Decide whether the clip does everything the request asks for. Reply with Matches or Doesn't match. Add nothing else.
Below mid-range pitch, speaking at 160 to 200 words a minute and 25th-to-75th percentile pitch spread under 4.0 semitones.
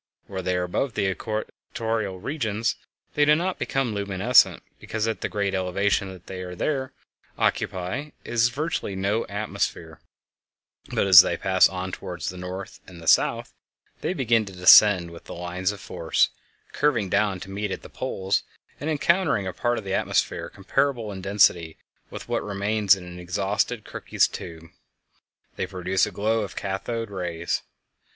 Matches